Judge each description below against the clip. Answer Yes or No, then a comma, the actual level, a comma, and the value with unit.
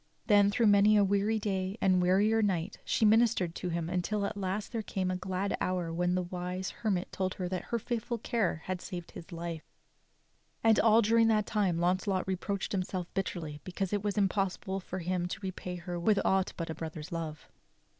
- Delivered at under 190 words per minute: No, fast, 205 wpm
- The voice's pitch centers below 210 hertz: Yes, high, 190 Hz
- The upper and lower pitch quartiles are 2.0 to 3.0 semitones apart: Yes, narrow, 2.5 semitones